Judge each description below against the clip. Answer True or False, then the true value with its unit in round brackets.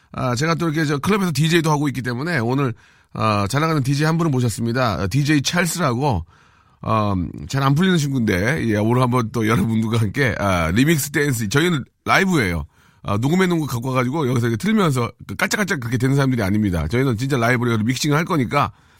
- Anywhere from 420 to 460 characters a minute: True (435 characters per minute)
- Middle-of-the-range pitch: False (130 Hz)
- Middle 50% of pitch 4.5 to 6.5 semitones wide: True (5.3 semitones)